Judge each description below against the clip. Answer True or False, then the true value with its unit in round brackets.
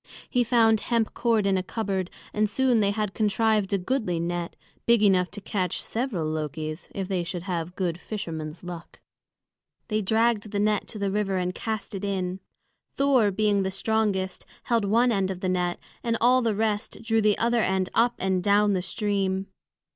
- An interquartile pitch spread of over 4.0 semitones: False (3.2 semitones)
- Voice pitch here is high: True (200 Hz)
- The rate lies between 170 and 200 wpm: True (185 wpm)